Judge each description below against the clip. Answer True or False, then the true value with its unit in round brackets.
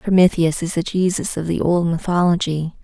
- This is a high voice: False (170 Hz)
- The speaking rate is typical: True (170 wpm)